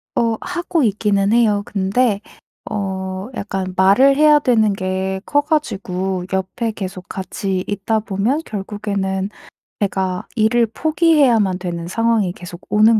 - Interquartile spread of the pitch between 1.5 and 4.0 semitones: Yes, average, 3.5 semitones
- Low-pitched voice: No, high, 205 Hz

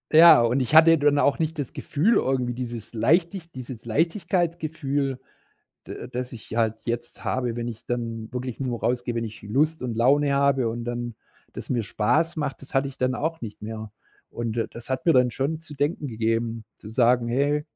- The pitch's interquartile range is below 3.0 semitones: No, average, 3.8 semitones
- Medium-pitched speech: No, low, 125 Hz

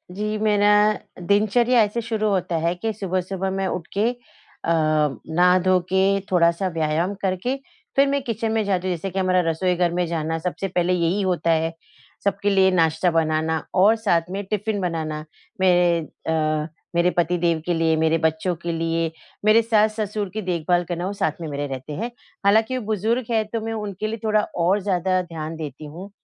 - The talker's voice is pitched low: No, medium, 185 Hz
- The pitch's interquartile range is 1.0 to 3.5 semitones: No, average, 4.1 semitones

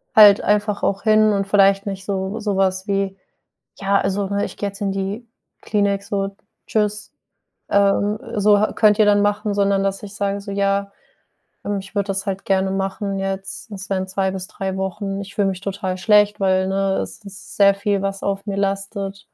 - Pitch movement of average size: No, narrow, 0.9 semitones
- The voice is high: Yes, high, 200 Hz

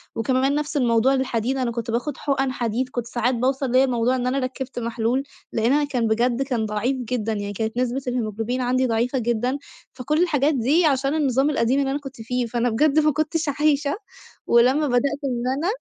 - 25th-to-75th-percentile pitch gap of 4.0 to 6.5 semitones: No, average, 2.7 semitones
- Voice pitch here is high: Yes, very high, 255 Hz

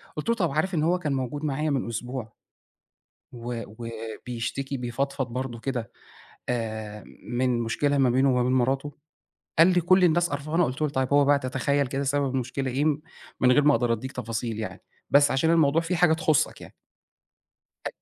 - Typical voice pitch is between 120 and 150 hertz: Yes, low, 135 Hz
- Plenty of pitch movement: No, average, 3.4 semitones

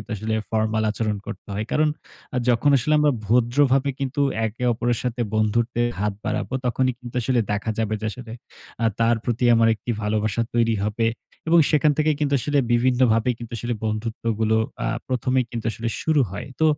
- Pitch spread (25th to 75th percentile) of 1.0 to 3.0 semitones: Yes, average, 2.7 semitones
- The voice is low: Yes, low, 120 Hz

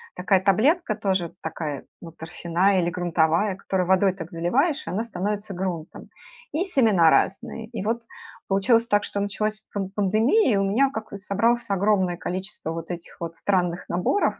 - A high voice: Yes, high, 195 Hz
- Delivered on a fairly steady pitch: No, average, 3.5 semitones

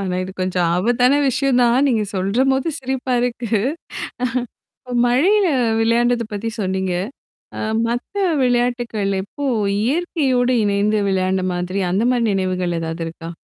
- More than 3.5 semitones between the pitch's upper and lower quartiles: Yes, average, 4.9 semitones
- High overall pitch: Yes, high, 230 Hz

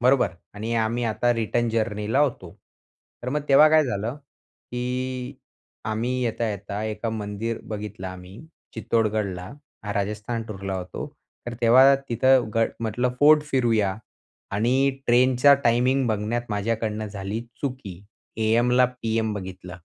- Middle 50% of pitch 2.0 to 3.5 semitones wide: Yes, average, 2.9 semitones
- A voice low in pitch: Yes, low, 115 Hz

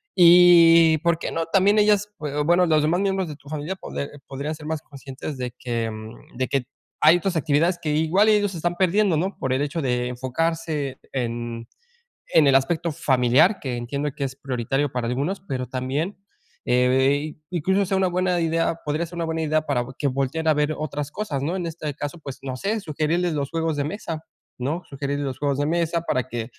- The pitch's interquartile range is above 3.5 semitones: Yes, average, 4.1 semitones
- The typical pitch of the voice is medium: Yes, medium, 155 Hz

